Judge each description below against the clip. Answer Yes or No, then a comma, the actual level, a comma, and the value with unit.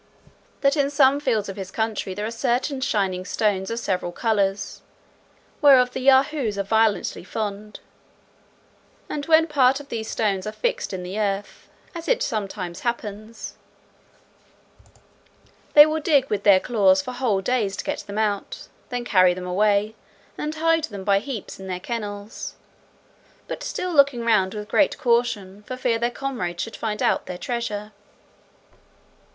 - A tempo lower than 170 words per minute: Yes, average, 155 wpm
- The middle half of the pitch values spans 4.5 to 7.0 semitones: Yes, average, 4.8 semitones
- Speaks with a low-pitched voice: No, high, 220 Hz